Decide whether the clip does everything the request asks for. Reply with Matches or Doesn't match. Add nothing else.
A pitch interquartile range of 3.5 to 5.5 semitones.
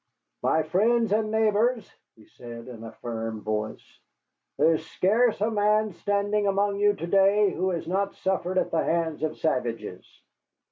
Matches